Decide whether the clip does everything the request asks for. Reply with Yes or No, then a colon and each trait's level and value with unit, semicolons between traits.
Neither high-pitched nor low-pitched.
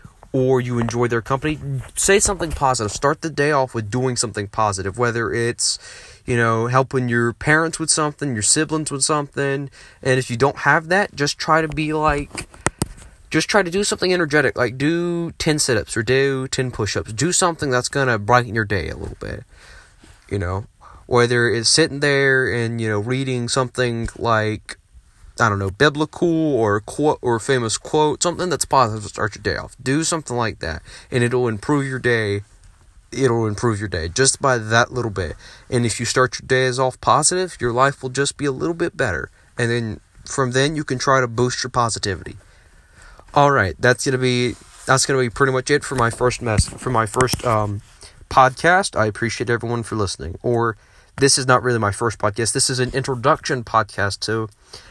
No: low, 125 Hz